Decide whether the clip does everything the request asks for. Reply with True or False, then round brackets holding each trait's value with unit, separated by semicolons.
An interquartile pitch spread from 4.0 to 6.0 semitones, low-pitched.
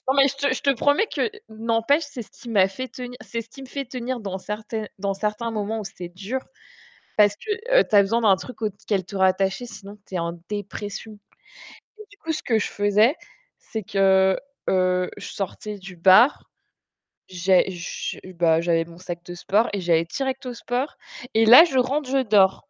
False (4.5 semitones; 210 Hz)